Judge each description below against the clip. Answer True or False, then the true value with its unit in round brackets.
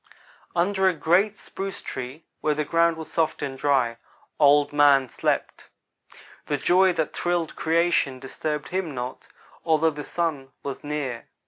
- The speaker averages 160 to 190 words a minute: False (145 wpm)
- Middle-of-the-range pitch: True (150 Hz)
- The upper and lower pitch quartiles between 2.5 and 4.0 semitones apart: True (3.4 semitones)